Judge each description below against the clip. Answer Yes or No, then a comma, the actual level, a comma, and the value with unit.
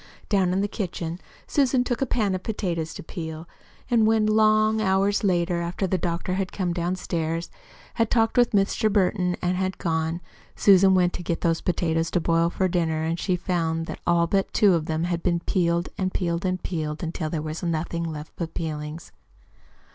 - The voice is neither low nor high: Yes, medium, 175 Hz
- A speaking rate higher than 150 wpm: Yes, average, 190 wpm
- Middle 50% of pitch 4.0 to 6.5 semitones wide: No, average, 2.8 semitones